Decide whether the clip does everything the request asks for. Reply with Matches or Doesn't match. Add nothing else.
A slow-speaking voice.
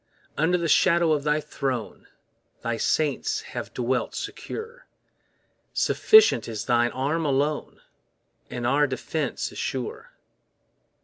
Matches